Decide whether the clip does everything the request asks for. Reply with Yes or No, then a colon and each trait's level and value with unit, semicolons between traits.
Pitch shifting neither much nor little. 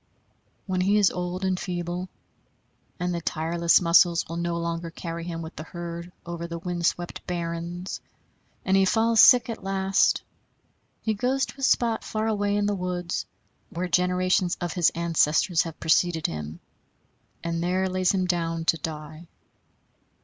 No: narrow, 2.0 semitones